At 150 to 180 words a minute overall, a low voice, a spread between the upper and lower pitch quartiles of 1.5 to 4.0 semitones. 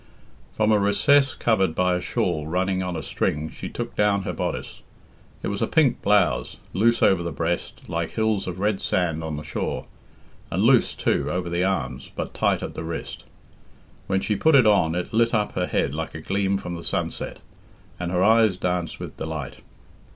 No: average, 195 wpm; very low, 95 Hz; average, 3.7 semitones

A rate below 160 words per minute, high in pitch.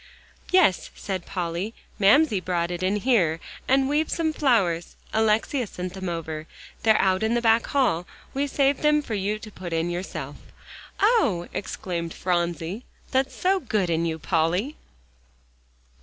Yes: average, 150 wpm; high, 195 Hz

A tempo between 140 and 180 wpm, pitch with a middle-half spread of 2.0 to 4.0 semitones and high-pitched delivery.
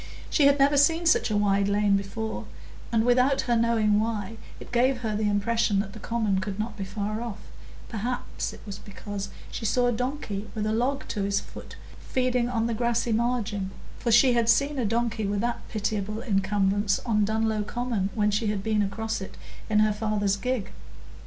No: average, 195 wpm; average, 2.7 semitones; high, 220 Hz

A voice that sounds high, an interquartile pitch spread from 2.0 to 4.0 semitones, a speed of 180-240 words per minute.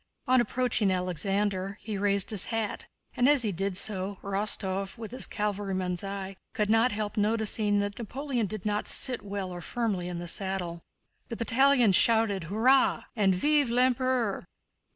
No: high, 205 Hz; average, 3.2 semitones; average, 155 wpm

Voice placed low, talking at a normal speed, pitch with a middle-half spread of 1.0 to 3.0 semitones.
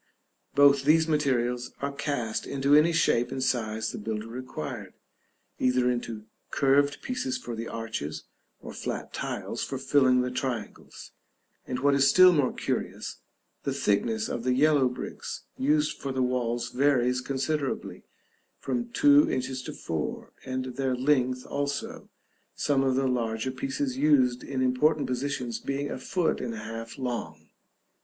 Yes: low, 130 Hz; average, 150 wpm; narrow, 2.6 semitones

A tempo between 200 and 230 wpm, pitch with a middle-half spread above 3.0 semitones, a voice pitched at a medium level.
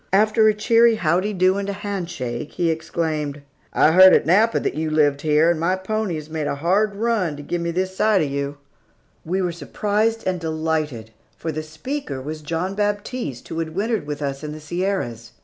Yes: fast, 205 wpm; average, 4.7 semitones; medium, 170 Hz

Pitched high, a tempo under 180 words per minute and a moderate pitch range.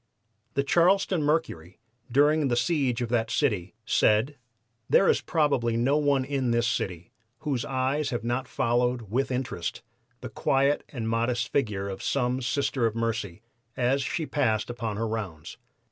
No: low, 125 Hz; average, 155 wpm; average, 3.7 semitones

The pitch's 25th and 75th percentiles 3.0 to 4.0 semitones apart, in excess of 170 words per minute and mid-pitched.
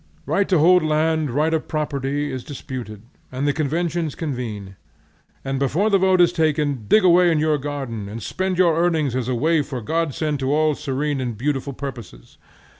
Yes: average, 3.7 semitones; average, 185 wpm; medium, 150 Hz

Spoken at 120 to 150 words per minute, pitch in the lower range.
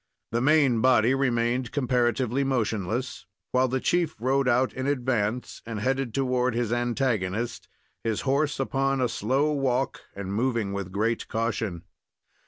Yes: average, 140 wpm; low, 125 Hz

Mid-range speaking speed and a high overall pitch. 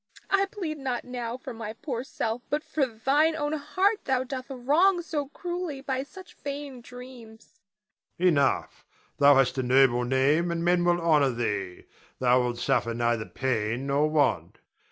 Yes: average, 165 wpm; high, 230 Hz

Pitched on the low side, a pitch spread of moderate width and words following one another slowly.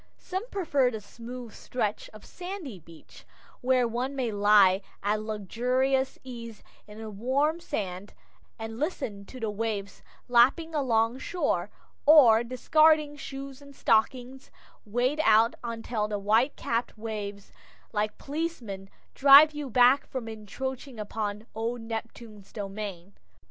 No: high, 235 Hz; average, 4.1 semitones; slow, 130 wpm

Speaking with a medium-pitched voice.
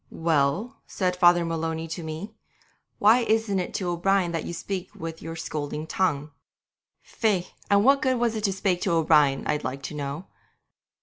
Yes: medium, 175 Hz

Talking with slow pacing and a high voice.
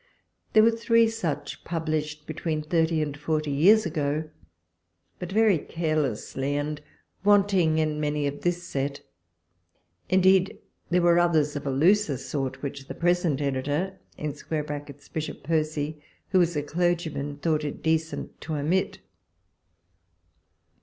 No: slow, 125 wpm; medium, 155 Hz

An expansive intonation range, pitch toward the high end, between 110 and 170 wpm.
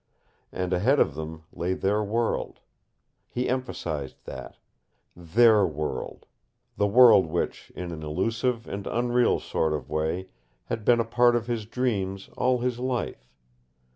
No: wide, 5.9 semitones; low, 105 Hz; average, 140 wpm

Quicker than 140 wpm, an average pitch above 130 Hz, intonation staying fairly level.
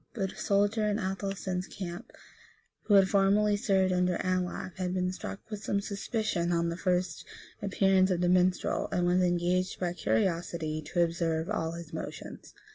Yes: average, 165 wpm; medium, 185 Hz; narrow, 2.0 semitones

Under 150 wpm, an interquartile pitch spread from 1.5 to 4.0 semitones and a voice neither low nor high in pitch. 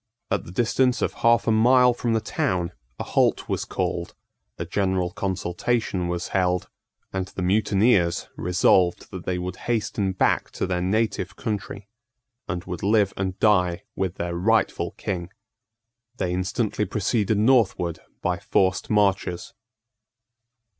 No: average, 140 wpm; average, 3.4 semitones; very low, 95 Hz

